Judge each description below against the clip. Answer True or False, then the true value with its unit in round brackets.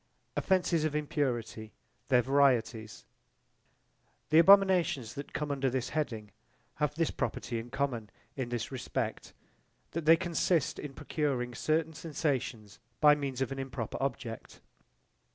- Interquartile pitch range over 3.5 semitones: True (4.2 semitones)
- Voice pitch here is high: False (135 Hz)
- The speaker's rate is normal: False (130 wpm)